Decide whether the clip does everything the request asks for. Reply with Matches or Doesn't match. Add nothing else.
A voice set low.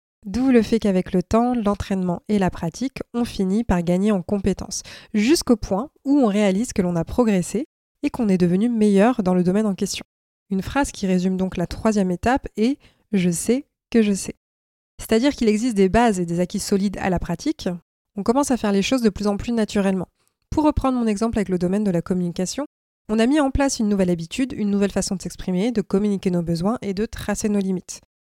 Doesn't match